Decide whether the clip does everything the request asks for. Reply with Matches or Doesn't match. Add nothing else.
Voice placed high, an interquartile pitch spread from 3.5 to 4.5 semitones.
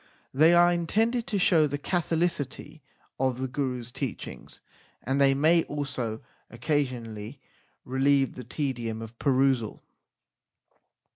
Doesn't match